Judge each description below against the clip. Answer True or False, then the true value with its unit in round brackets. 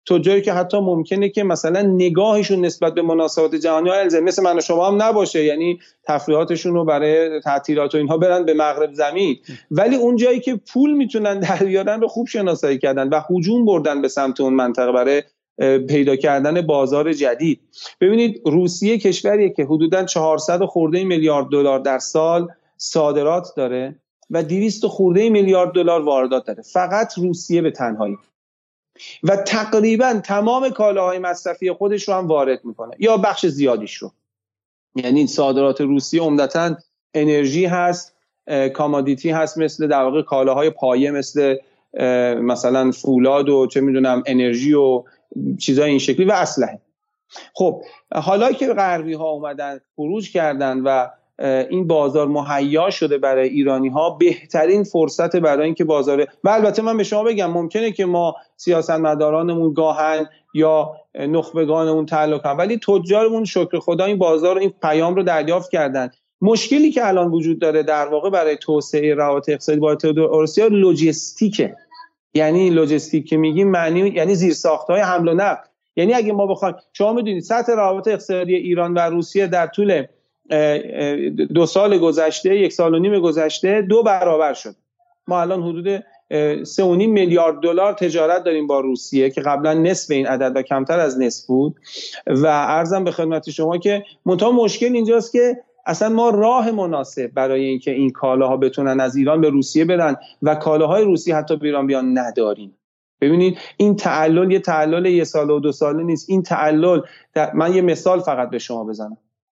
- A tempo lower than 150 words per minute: False (155 wpm)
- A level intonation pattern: False (4.6 semitones)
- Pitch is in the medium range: True (165 Hz)